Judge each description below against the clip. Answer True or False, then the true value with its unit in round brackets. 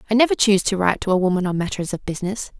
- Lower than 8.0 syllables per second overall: False (8.1 syllables/s)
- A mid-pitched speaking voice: False (200 Hz)